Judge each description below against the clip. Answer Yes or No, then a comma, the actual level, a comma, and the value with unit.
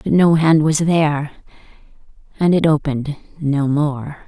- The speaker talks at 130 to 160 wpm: Yes, average, 140 wpm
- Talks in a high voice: No, medium, 150 Hz